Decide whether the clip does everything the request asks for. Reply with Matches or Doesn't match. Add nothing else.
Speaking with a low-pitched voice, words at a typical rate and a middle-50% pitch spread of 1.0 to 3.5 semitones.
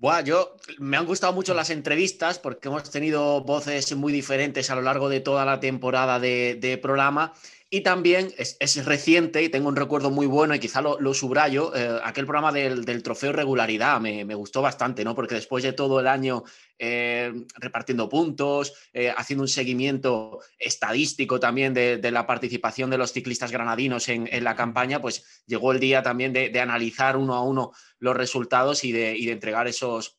Doesn't match